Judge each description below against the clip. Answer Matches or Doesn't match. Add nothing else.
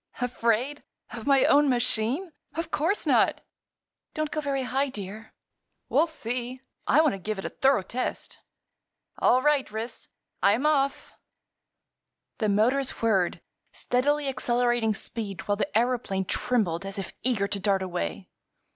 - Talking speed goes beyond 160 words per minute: Doesn't match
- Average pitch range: Matches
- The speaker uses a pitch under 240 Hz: Doesn't match